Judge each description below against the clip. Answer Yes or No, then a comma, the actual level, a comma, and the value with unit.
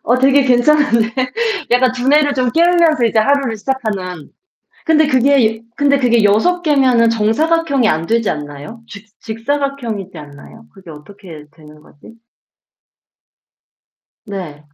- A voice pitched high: Yes, high, 230 Hz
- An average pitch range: No, wide, 5.8 semitones